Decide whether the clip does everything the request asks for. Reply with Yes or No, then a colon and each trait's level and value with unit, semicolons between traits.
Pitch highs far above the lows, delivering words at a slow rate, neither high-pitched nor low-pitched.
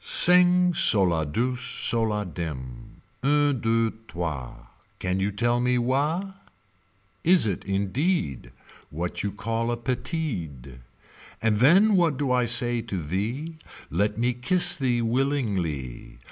No: wide, 7.0 semitones; slow, 130 wpm; low, 115 Hz